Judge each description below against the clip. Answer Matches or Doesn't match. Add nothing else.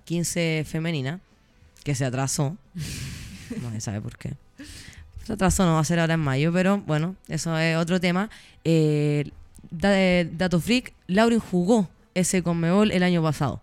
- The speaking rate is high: Doesn't match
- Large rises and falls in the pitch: Doesn't match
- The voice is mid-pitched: Matches